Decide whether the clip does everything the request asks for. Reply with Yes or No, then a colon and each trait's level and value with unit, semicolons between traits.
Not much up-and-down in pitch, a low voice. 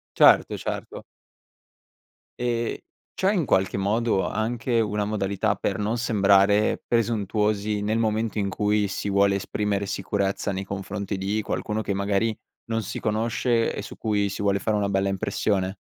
Yes: narrow, 1.8 semitones; low, 105 Hz